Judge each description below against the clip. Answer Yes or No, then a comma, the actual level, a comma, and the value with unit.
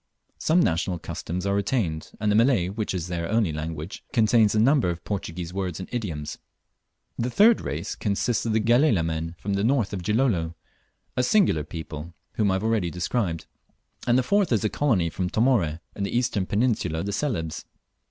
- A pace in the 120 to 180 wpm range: No, average, 190 wpm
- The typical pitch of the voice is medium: No, low, 100 Hz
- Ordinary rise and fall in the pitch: No, wide, 5.7 semitones